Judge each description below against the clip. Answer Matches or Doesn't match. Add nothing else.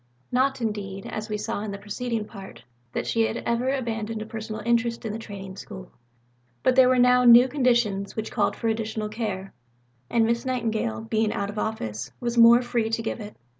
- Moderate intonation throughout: Doesn't match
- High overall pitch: Matches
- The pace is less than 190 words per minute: Doesn't match